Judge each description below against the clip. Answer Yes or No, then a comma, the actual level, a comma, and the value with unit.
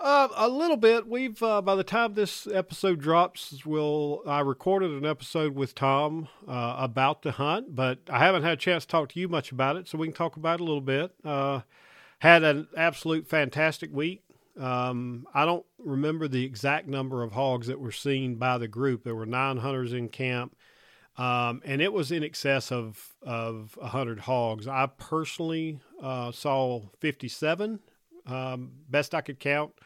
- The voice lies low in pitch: No, medium, 145 Hz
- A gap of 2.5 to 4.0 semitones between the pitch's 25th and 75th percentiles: No, average, 4.4 semitones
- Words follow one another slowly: No, average, 185 wpm